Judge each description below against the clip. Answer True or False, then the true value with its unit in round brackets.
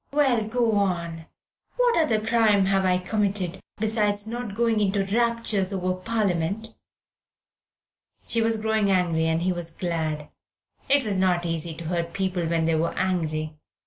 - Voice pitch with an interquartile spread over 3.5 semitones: True (4.5 semitones)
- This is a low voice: False (195 Hz)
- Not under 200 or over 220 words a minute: False (155 wpm)